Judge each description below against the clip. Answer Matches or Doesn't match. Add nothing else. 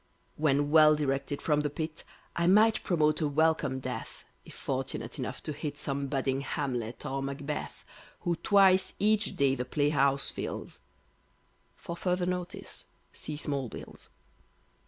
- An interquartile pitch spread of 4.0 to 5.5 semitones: Doesn't match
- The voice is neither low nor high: Matches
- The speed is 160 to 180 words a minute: Doesn't match